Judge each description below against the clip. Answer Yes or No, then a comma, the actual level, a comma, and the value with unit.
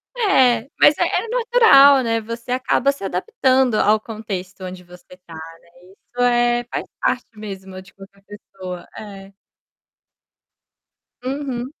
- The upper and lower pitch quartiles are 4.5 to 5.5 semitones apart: Yes, average, 5.1 semitones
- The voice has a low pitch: No, high, 225 Hz